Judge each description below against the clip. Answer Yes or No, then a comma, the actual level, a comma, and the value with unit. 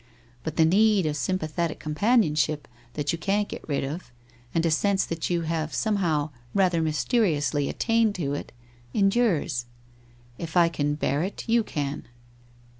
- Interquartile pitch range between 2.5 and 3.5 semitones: No, average, 4.8 semitones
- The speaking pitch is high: No, medium, 165 Hz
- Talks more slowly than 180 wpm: Yes, average, 150 wpm